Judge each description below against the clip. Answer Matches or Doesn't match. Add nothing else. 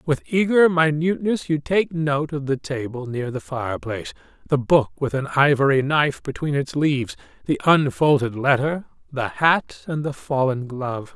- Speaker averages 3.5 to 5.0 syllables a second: Matches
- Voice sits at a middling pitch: Matches